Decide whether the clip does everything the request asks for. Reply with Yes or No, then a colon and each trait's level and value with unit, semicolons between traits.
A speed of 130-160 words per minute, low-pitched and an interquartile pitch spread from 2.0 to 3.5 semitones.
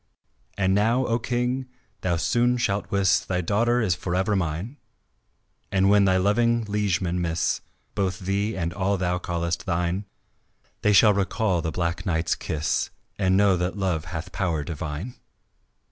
Yes: average, 150 wpm; very low, 95 Hz; average, 3.1 semitones